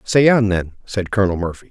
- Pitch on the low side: Yes, low, 100 Hz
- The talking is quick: Yes, fast, 210 wpm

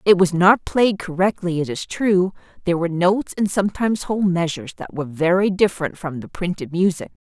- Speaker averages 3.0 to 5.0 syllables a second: No, 6.0 syllables/s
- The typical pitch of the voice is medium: Yes, medium, 180 Hz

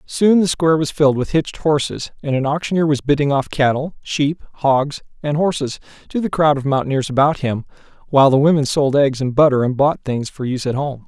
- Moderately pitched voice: Yes, medium, 145 Hz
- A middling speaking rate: No, fast, 215 wpm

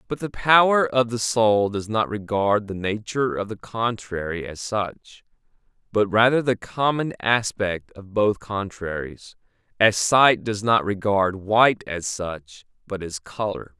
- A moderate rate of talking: Yes, average, 150 wpm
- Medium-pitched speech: No, low, 105 Hz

